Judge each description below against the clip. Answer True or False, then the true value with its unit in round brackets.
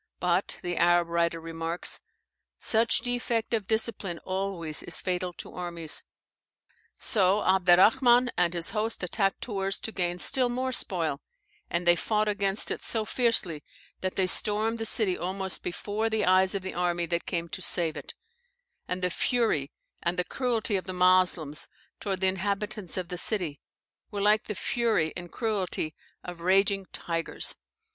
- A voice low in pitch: False (185 Hz)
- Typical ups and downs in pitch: True (3.6 semitones)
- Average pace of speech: True (160 wpm)